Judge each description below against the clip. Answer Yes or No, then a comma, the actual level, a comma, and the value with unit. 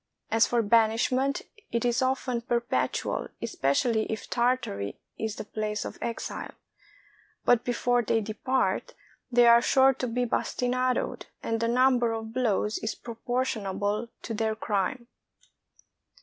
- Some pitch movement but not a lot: No, narrow, 2.2 semitones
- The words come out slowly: Yes, slow, 130 wpm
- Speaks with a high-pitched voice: Yes, high, 235 Hz